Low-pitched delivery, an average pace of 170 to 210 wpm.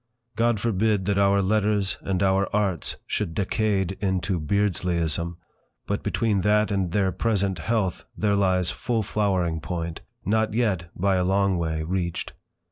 No: very low, 95 Hz; average, 145 wpm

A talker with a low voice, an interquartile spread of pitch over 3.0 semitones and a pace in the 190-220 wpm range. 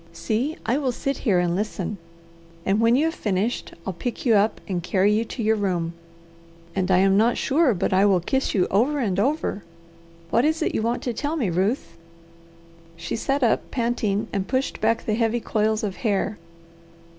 No: high, 215 Hz; average, 4.1 semitones; average, 195 wpm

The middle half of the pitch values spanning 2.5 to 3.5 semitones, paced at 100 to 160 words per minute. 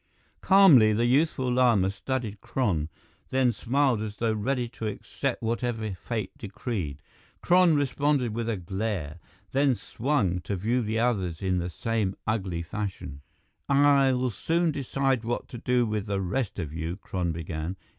No: average, 5.1 semitones; average, 150 wpm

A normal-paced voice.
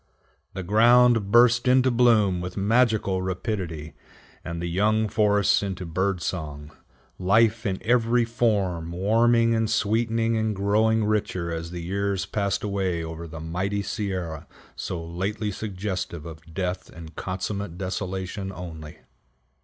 No: slow, 130 wpm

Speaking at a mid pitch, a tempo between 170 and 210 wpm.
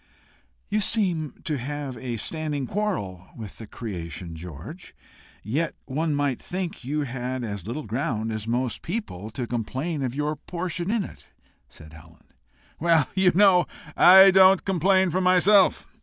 No: medium, 145 Hz; average, 150 wpm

